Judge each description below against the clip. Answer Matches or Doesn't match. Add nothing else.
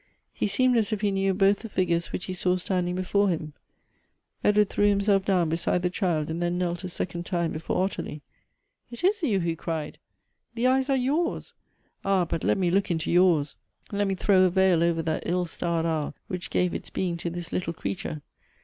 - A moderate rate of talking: Doesn't match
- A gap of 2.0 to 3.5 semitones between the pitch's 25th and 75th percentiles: Matches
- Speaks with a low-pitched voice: Doesn't match